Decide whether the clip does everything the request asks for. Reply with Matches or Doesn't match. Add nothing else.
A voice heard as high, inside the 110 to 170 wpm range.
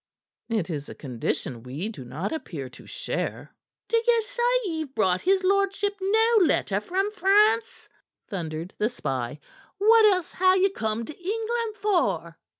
Matches